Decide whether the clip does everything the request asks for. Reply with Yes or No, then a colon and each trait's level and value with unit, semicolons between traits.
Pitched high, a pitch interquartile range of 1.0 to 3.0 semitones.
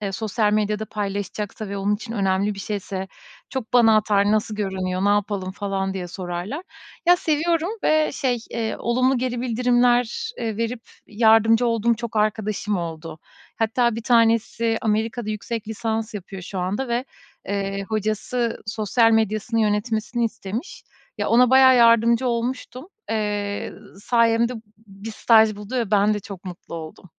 Yes: high, 220 Hz; narrow, 2.6 semitones